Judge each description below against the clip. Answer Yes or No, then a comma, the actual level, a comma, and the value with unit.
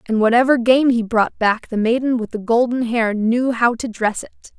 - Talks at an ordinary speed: No, fast, 225 wpm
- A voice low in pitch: No, high, 235 Hz